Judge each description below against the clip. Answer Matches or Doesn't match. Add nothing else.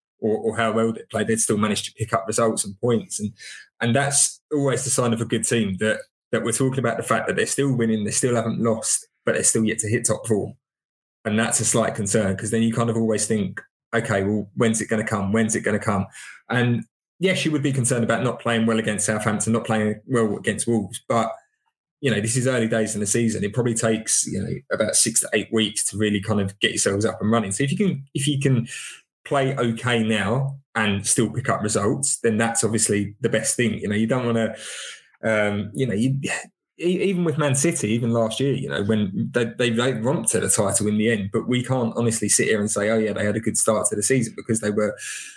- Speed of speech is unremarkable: Doesn't match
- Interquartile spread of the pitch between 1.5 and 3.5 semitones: Matches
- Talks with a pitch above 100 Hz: Matches